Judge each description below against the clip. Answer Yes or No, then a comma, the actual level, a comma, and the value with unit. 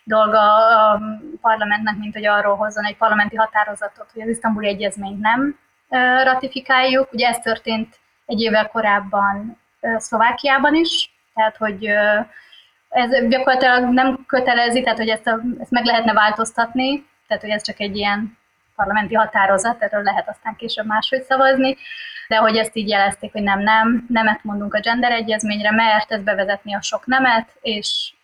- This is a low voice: No, high, 220 Hz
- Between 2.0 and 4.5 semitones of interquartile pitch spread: Yes, average, 2.9 semitones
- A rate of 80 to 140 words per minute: No, fast, 155 wpm